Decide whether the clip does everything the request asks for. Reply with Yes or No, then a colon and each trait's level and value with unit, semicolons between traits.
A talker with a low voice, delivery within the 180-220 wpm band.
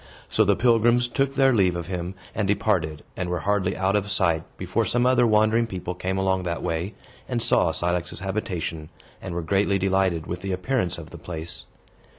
Yes: very low, 95 Hz; average, 190 wpm